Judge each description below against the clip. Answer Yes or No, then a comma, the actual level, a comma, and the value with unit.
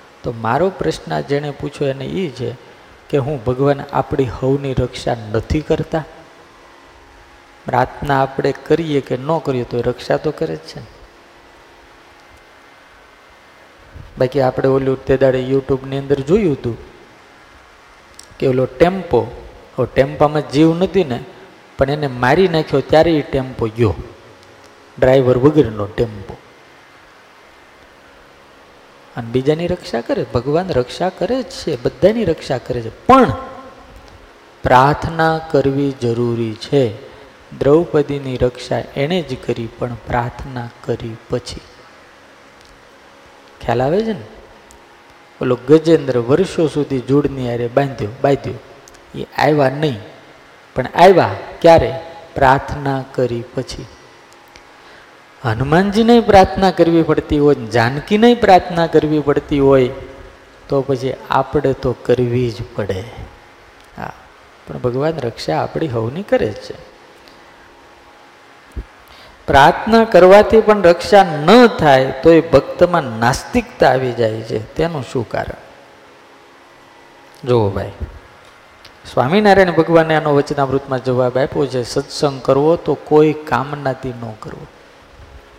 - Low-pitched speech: Yes, low, 130 Hz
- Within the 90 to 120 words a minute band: Yes, average, 115 wpm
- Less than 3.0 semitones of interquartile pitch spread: No, wide, 5.4 semitones